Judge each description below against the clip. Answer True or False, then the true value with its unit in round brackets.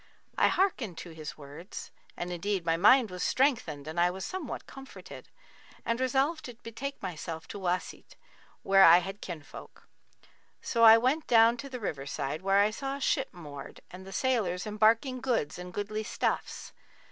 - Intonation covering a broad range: True (6.2 semitones)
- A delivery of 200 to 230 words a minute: False (170 wpm)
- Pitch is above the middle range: True (205 Hz)